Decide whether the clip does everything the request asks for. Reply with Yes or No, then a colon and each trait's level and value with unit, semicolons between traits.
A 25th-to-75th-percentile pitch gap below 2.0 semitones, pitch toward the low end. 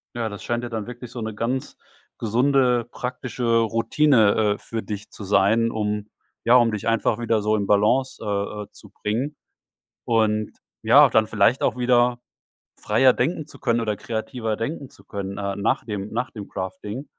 No: narrow, 2.6 semitones; low, 115 Hz